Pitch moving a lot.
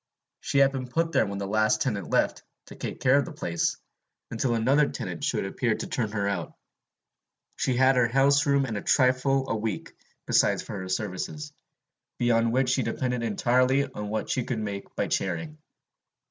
No: average, 3.9 semitones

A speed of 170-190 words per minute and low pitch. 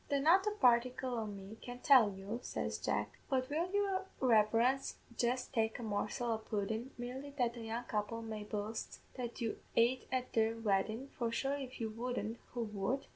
No: average, 185 wpm; high, 235 Hz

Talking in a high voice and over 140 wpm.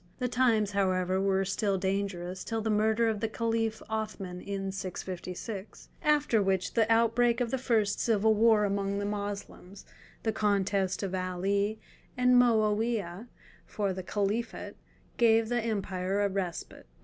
No: high, 205 Hz; slow, 135 wpm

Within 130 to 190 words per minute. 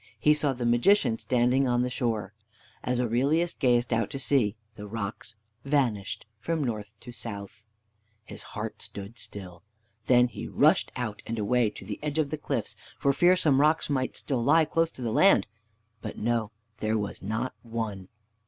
Yes: average, 175 wpm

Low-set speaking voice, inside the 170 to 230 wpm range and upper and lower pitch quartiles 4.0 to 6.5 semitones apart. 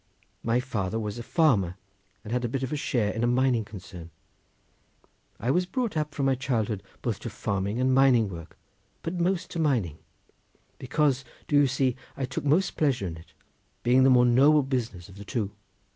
Yes: low, 125 Hz; average, 190 wpm; average, 4.8 semitones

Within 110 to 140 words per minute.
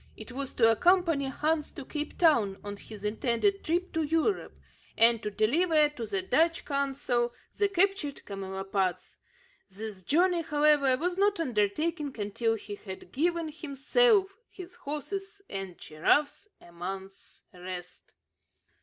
Yes: slow, 135 wpm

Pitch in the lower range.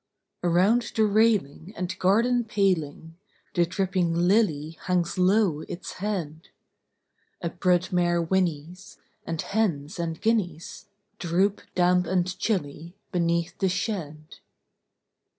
No: medium, 180 Hz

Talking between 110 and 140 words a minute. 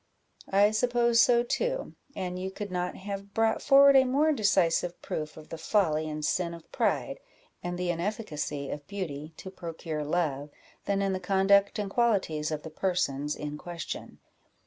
No: average, 170 wpm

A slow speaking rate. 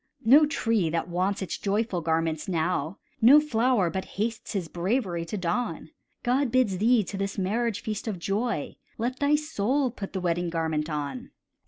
No: average, 170 wpm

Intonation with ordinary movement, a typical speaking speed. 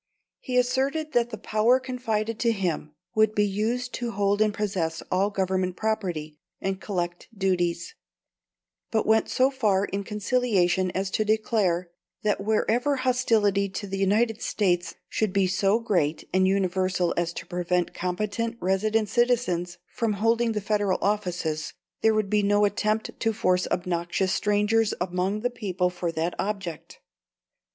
Yes: average, 3.3 semitones; average, 150 wpm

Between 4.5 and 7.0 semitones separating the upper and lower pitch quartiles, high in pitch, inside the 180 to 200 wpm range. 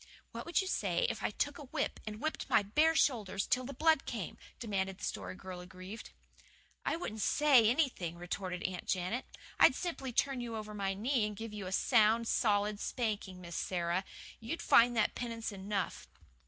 Yes: average, 4.8 semitones; high, 215 Hz; average, 185 wpm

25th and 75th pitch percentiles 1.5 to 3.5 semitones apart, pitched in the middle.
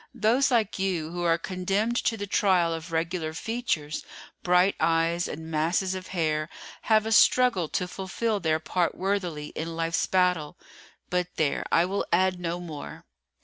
Yes: average, 2.9 semitones; medium, 180 Hz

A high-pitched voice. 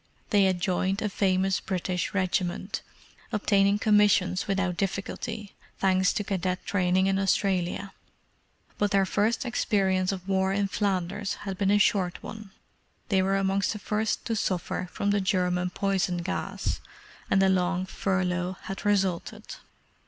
Yes: high, 195 Hz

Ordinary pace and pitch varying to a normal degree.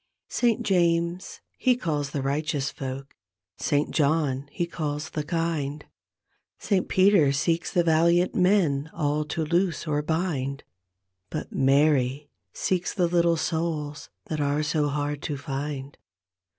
No: slow, 130 wpm; average, 3.1 semitones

